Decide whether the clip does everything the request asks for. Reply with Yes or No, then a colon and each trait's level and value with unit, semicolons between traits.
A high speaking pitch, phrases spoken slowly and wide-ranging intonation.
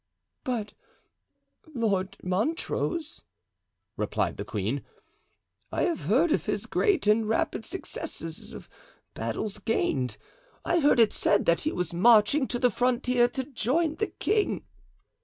Yes: high, 235 Hz; slow, 130 wpm; wide, 6.7 semitones